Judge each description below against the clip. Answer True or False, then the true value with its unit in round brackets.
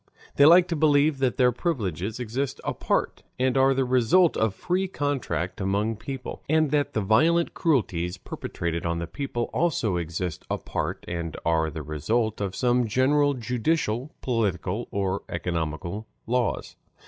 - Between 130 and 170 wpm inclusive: True (150 wpm)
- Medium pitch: False (115 Hz)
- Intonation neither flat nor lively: False (7.4 semitones)